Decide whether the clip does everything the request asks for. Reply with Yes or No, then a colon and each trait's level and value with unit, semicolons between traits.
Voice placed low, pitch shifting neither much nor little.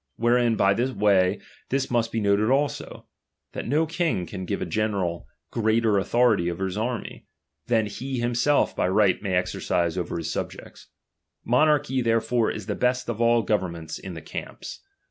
Yes: low, 110 Hz; average, 4.3 semitones